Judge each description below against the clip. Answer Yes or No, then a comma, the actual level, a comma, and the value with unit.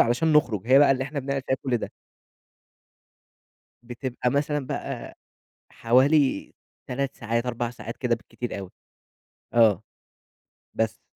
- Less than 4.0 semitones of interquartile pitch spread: Yes, average, 2.9 semitones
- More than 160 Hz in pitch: No, low, 125 Hz